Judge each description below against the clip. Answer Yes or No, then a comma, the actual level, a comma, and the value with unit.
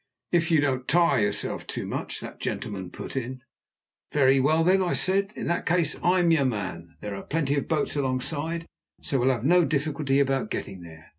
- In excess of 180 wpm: Yes, average, 195 wpm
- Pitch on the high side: No, medium, 140 Hz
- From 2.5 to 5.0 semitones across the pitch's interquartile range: Yes, average, 4.5 semitones